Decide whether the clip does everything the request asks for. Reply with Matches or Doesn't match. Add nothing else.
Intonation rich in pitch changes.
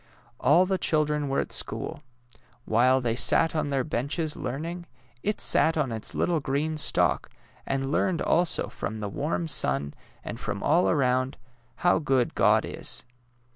Doesn't match